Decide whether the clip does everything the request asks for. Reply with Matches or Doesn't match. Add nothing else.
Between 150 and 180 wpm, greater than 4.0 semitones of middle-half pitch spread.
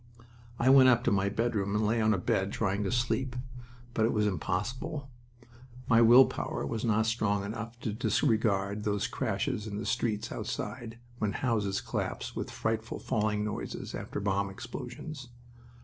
Doesn't match